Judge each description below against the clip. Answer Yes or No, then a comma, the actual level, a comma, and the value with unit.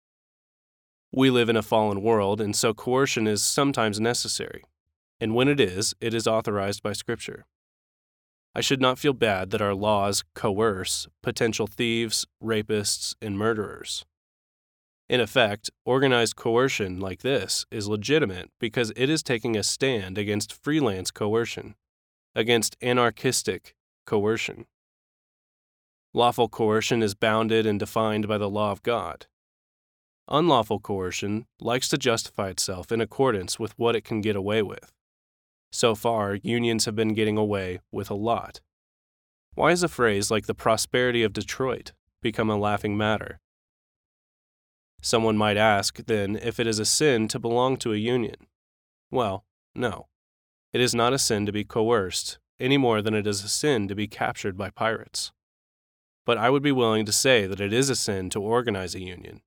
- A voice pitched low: Yes, low, 110 Hz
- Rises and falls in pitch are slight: No, average, 3.1 semitones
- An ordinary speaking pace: Yes, average, 155 wpm